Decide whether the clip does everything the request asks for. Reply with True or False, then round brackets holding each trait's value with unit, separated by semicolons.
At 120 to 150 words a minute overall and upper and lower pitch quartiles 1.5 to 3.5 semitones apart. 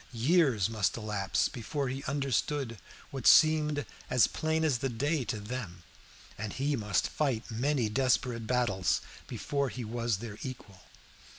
False (140 wpm; 4.4 semitones)